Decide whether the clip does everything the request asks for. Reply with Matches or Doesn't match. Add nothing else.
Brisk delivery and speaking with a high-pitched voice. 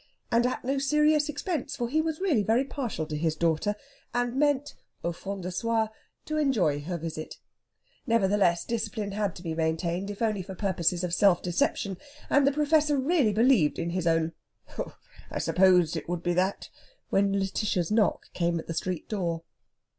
Doesn't match